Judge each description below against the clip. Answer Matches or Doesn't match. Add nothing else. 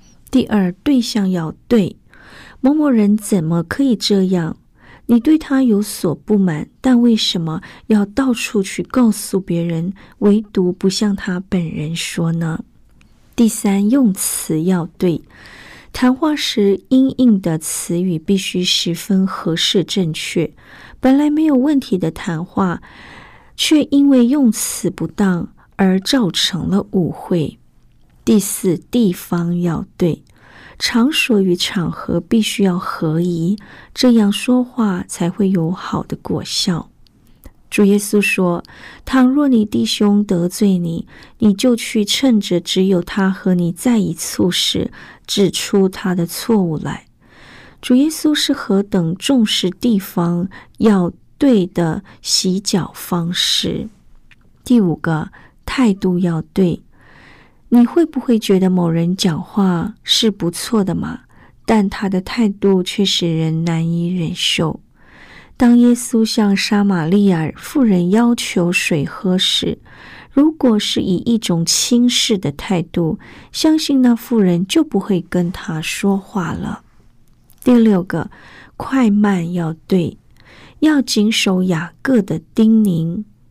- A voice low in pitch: Doesn't match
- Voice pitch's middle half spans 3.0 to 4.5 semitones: Doesn't match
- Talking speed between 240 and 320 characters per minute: Doesn't match